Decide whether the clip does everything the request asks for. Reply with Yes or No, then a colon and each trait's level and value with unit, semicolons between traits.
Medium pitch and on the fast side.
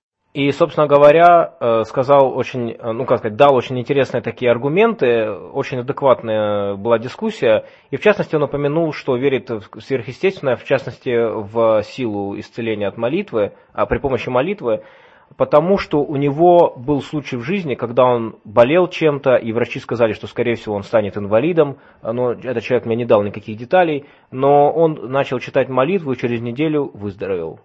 No: low, 130 Hz; fast, 165 wpm